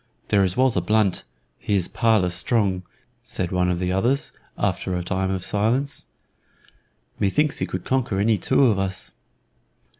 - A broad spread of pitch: No, average, 3.9 semitones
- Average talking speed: Yes, average, 155 wpm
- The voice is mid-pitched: No, low, 100 Hz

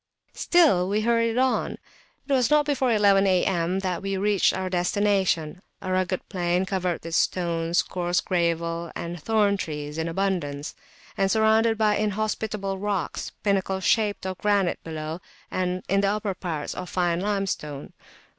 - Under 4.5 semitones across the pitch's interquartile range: Yes, average, 3.2 semitones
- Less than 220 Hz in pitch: Yes, high, 190 Hz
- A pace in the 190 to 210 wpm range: No, average, 145 wpm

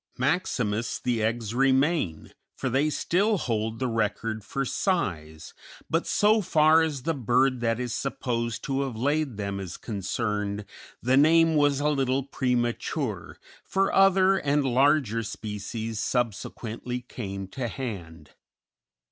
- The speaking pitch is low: Yes, low, 125 Hz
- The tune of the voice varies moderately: Yes, average, 4.7 semitones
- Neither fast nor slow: No, slow, 130 wpm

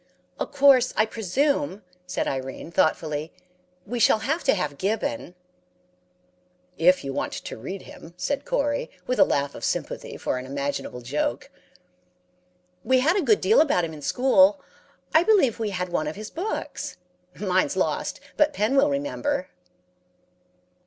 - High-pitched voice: Yes, high, 220 Hz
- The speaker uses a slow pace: No, average, 150 wpm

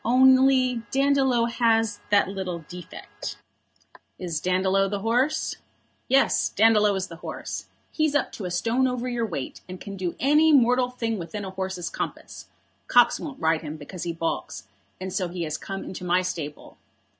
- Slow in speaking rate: No, average, 165 wpm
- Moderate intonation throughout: No, wide, 5.7 semitones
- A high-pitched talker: Yes, high, 205 Hz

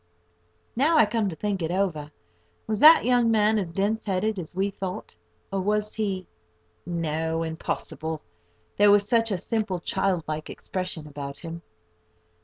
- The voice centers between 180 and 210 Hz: Yes, high, 190 Hz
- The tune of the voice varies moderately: Yes, average, 4.6 semitones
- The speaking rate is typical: Yes, average, 150 wpm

